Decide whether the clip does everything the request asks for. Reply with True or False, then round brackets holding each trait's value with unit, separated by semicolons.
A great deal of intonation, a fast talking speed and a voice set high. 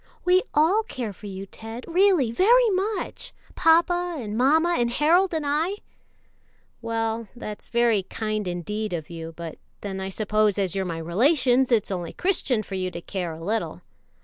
False (8.8 semitones; 170 wpm; 225 Hz)